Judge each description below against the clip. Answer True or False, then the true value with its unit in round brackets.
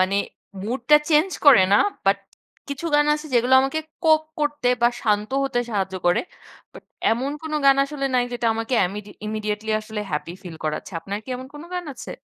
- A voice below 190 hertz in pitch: False (240 Hz)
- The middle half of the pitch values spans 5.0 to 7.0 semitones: True (5.4 semitones)